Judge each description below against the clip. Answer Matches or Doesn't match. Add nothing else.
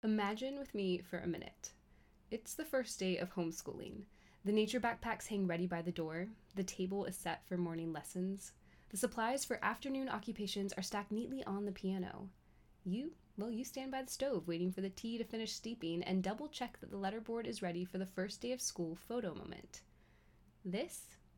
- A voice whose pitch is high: Matches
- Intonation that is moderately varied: Matches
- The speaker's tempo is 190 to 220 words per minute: Matches